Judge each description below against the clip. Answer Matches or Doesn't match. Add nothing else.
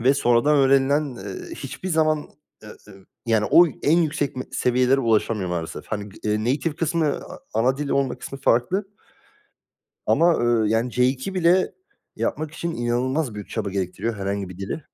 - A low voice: Matches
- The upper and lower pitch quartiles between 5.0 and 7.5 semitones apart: Matches